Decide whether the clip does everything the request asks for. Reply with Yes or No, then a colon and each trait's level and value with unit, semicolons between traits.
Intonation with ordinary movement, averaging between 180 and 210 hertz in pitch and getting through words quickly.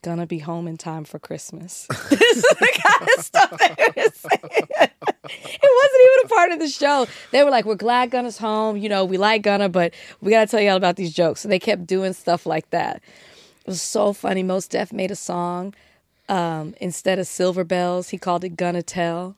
Yes: average, 3.9 semitones; high, 190 Hz; fast, 210 wpm